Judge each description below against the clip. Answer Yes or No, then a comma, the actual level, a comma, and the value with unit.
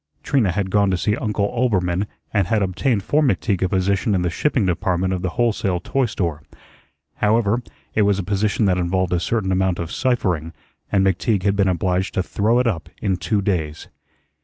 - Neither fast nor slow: Yes, average, 195 wpm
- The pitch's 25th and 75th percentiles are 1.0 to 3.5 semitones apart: Yes, average, 2.9 semitones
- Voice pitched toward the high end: No, very low, 95 Hz